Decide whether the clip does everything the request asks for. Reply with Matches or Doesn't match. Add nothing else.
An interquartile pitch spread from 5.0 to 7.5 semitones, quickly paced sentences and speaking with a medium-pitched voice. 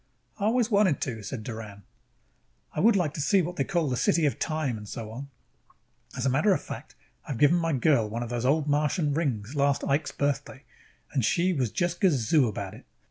Matches